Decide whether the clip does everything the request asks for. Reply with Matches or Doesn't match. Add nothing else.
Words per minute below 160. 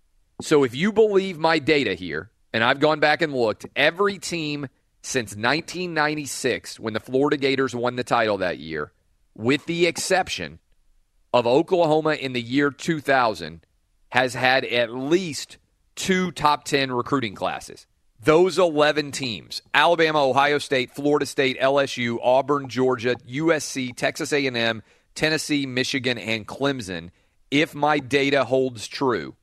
Matches